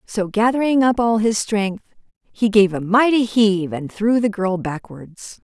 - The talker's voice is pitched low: No, high, 210 Hz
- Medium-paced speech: Yes, average, 175 wpm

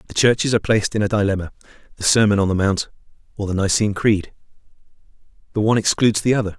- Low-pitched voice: Yes, low, 105 Hz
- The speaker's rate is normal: Yes, average, 180 wpm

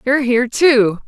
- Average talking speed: Yes, average, 170 wpm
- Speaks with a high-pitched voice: Yes, very high, 250 Hz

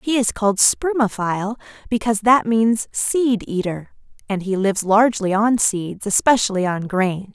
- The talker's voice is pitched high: Yes, high, 215 Hz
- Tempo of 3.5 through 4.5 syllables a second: No, 4.8 syllables/s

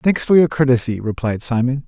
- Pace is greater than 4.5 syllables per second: Yes, 5.5 syllables/s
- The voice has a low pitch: Yes, low, 130 Hz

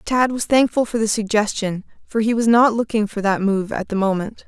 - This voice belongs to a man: No, female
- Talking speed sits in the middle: No, fast, 230 wpm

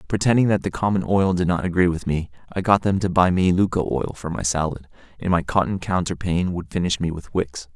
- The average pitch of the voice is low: Yes, very low, 90 Hz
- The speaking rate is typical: No, fast, 230 wpm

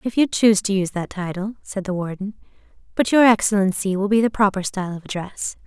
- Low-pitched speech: No, high, 200 Hz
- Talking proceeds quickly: Yes, fast, 210 wpm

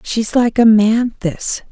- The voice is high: Yes, high, 215 Hz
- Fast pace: No, slow, 105 wpm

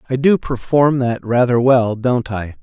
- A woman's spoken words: No, male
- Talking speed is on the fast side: No, average, 185 wpm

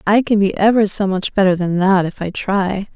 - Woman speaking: Yes, female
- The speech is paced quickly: Yes, fast, 245 wpm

